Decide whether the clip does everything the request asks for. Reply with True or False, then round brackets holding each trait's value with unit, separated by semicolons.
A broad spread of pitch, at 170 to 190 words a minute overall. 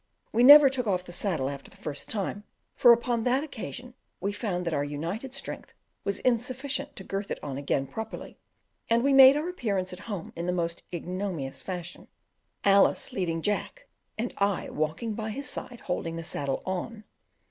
True (5.9 semitones; 180 wpm)